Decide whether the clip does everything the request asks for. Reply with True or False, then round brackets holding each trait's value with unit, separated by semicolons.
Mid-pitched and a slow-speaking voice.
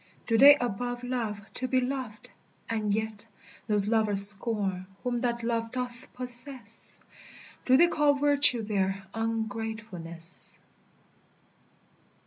False (230 Hz; 115 wpm)